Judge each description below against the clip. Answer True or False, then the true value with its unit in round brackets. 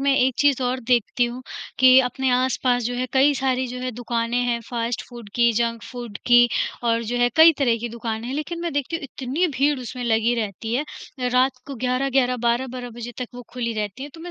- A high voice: True (245 Hz)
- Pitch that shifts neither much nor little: False (1.9 semitones)